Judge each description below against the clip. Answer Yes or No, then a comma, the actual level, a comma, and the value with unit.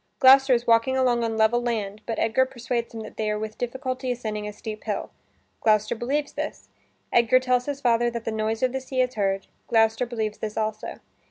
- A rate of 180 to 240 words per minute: Yes, fast, 205 wpm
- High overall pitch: Yes, high, 235 Hz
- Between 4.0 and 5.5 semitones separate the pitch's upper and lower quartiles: No, average, 2.7 semitones